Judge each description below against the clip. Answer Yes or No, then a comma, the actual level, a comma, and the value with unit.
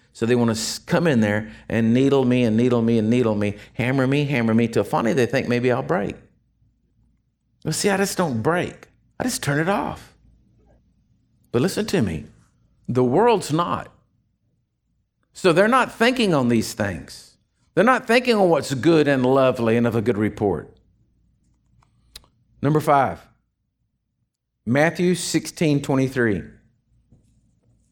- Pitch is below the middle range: Yes, low, 125 Hz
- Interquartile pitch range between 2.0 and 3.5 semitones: No, average, 5.2 semitones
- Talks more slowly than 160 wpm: Yes, average, 150 wpm